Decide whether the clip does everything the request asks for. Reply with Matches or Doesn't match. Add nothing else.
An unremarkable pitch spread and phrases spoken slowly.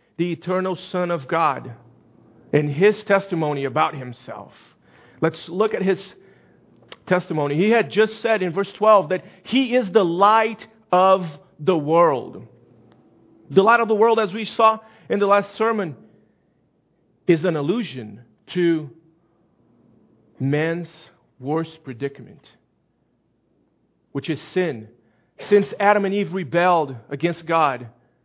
Doesn't match